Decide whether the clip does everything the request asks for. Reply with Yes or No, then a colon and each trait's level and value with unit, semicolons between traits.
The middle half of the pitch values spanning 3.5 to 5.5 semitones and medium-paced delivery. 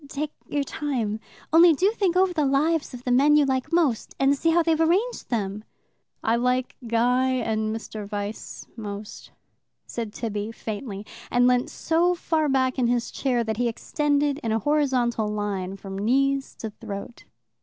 Yes: average, 5.1 semitones; average, 170 wpm